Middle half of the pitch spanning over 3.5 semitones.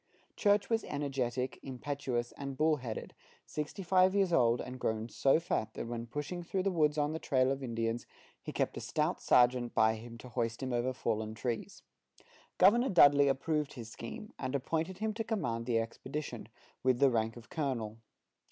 Yes: average, 5.1 semitones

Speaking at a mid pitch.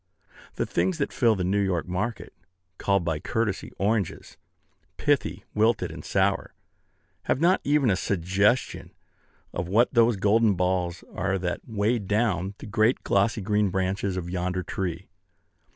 No: low, 100 Hz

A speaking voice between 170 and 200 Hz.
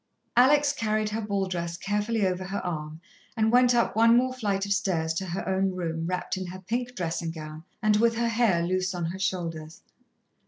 Yes: high, 190 Hz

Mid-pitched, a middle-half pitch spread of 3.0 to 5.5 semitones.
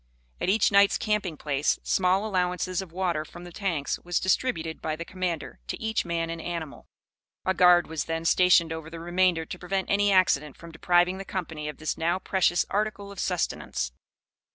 No: medium, 175 Hz; narrow, 2.6 semitones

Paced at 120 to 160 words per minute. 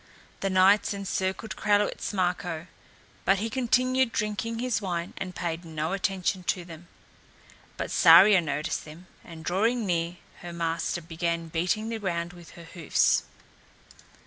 Yes: average, 140 wpm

